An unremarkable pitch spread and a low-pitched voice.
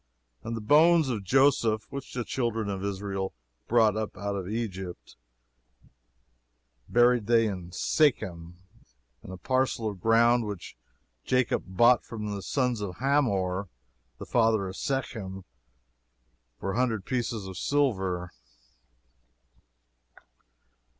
Yes: average, 4.2 semitones; low, 110 Hz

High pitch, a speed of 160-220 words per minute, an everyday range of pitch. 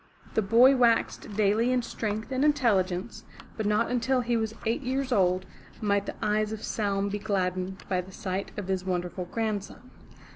Yes: high, 210 Hz; average, 175 wpm; average, 3.5 semitones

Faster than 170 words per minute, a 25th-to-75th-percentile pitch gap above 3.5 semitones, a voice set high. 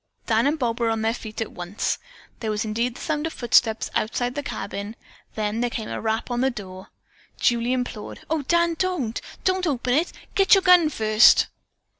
Yes: average, 195 wpm; average, 5.1 semitones; high, 240 Hz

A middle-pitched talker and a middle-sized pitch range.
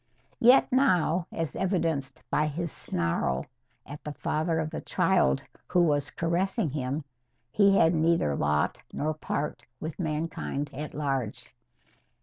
Yes: medium, 155 Hz; average, 3.1 semitones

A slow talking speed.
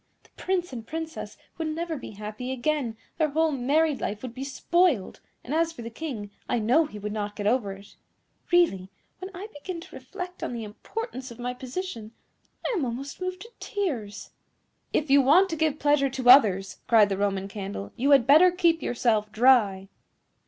No: average, 190 wpm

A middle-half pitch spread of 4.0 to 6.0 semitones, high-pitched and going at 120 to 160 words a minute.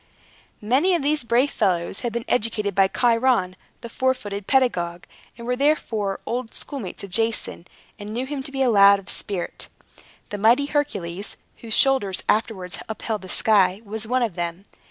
No: average, 4.3 semitones; high, 220 Hz; average, 175 wpm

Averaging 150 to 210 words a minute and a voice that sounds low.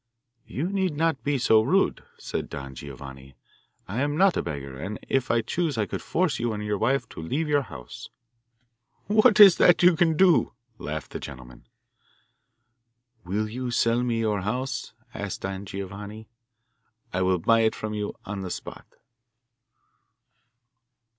Yes: average, 160 wpm; low, 110 Hz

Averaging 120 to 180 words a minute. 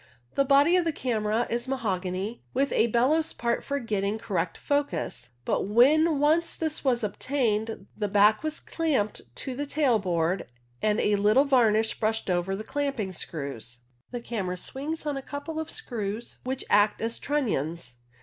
Yes: average, 165 wpm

